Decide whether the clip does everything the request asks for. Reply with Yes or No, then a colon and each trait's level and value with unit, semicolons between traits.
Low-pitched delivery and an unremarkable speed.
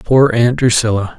Yes: low, 120 Hz; average, 150 wpm